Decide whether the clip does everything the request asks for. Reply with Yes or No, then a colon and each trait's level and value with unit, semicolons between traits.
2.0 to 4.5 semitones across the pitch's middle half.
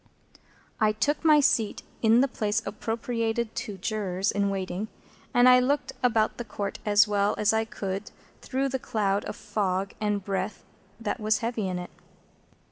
Yes: average, 2.7 semitones